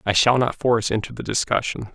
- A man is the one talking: Yes, male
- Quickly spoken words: Yes, fast, 215 wpm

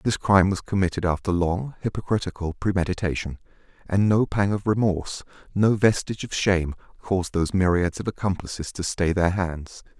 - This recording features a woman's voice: No, male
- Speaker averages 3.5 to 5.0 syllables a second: No, 5.7 syllables/s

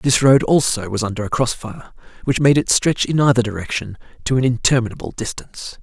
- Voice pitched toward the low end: Yes, low, 125 Hz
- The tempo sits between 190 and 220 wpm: Yes, average, 195 wpm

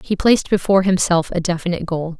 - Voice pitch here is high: No, medium, 180 Hz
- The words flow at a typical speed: Yes, average, 190 wpm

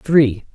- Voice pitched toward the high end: No, low, 135 Hz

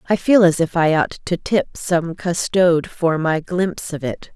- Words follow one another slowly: No, fast, 205 wpm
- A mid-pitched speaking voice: Yes, medium, 170 Hz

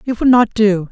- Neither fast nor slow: No, fast, 265 wpm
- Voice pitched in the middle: No, high, 220 Hz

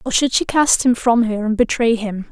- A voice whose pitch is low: No, high, 235 Hz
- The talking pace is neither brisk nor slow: No, fast, 260 wpm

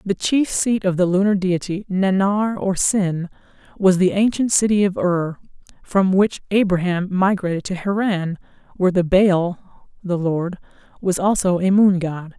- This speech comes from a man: No, female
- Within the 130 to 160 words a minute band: Yes, average, 155 wpm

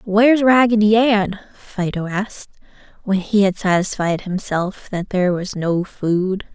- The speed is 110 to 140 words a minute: Yes, slow, 135 wpm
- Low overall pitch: No, high, 195 Hz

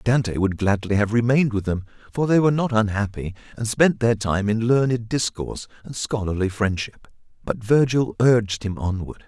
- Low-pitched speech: Yes, low, 110 Hz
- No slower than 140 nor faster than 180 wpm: Yes, average, 175 wpm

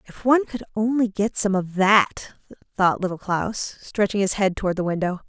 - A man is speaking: No, female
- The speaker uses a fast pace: No, average, 195 wpm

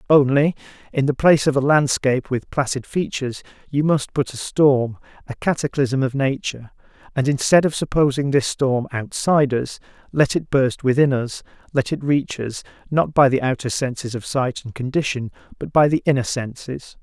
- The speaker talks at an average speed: Yes, average, 175 wpm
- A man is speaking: Yes, male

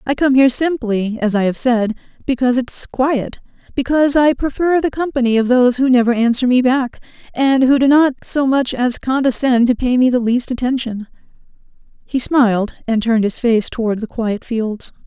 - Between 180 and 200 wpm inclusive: Yes, average, 185 wpm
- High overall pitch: Yes, very high, 250 Hz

